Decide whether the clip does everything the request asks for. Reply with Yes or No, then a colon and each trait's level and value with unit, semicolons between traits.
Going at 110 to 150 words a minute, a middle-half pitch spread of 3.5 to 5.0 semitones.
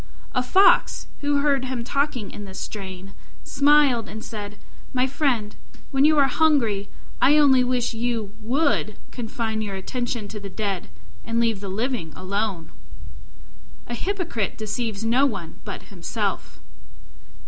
Yes: average, 140 wpm; average, 4.6 semitones